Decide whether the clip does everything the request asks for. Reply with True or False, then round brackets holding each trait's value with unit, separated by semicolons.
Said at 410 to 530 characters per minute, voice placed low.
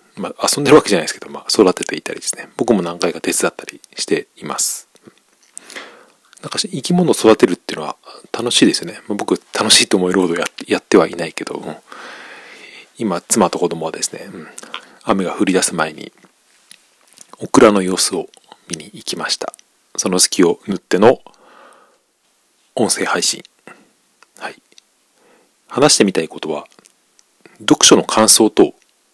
False (315 characters per minute; 110 Hz)